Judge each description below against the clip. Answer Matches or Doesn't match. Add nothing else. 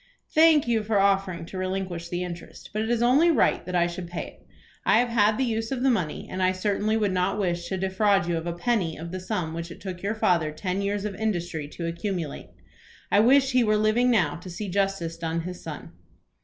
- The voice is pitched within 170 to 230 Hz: Matches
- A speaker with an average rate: Doesn't match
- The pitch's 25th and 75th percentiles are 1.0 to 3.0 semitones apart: Doesn't match